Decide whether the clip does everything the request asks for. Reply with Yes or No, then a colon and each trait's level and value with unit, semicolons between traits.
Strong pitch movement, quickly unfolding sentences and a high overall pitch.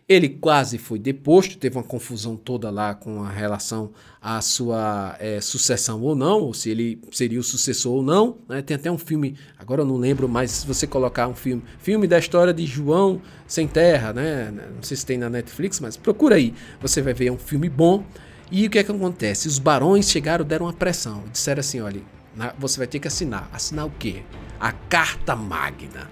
No: wide, 5.8 semitones; fast, 205 wpm; low, 130 Hz